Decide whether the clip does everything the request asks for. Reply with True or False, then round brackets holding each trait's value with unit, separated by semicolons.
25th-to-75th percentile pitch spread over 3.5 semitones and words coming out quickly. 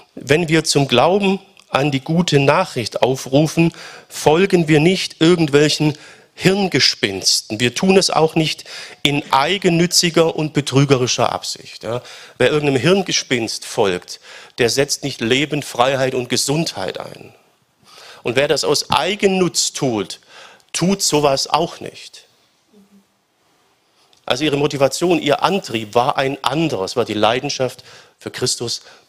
False (4.5 semitones; 125 wpm)